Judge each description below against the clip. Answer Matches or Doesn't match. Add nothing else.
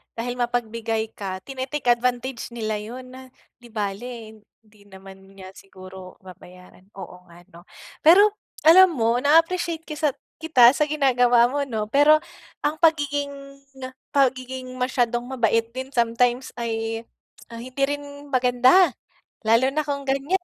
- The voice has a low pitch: Doesn't match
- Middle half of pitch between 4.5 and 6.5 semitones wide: Doesn't match